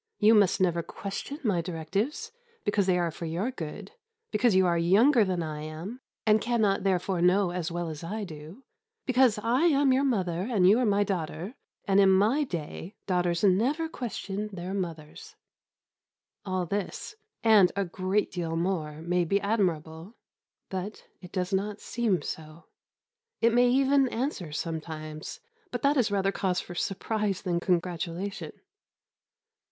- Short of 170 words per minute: Yes, average, 155 wpm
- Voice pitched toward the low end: No, high, 190 Hz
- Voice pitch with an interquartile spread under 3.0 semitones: No, average, 4.1 semitones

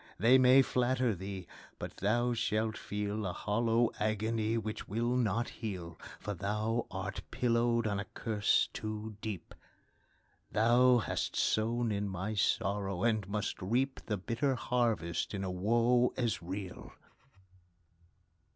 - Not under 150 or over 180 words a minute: No, slow, 135 wpm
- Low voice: Yes, low, 110 Hz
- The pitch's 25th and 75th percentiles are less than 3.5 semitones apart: Yes, average, 2.7 semitones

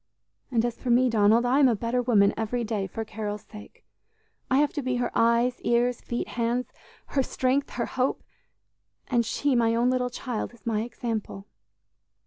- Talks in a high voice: Yes, high, 240 Hz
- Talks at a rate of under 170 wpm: No, average, 180 wpm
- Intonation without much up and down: Yes, narrow, 1.9 semitones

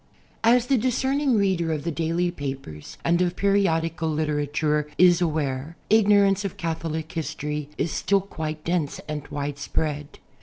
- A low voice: No, medium, 165 Hz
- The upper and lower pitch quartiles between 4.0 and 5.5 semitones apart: Yes, average, 4.4 semitones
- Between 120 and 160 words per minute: Yes, average, 145 wpm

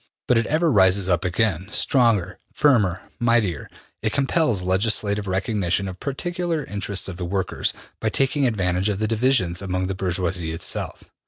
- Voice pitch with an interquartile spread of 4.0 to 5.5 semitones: Yes, average, 4.4 semitones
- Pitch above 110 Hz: No, low, 100 Hz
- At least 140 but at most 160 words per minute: Yes, average, 155 wpm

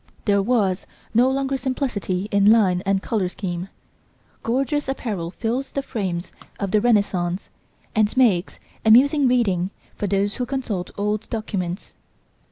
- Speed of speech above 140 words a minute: No, slow, 135 wpm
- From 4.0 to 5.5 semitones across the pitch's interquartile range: Yes, average, 4.8 semitones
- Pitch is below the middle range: No, high, 210 Hz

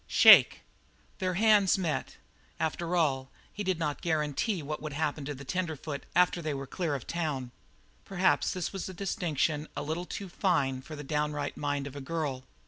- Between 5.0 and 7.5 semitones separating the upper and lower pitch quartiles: No, average, 3.7 semitones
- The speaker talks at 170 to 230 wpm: Yes, average, 190 wpm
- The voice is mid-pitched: Yes, medium, 155 Hz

